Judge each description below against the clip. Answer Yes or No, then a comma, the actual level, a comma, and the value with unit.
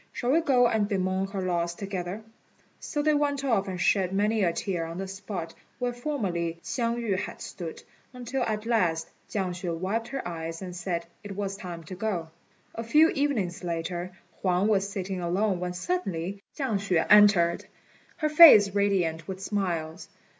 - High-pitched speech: Yes, high, 195 Hz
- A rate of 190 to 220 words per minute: No, average, 175 wpm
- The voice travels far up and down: No, average, 4.1 semitones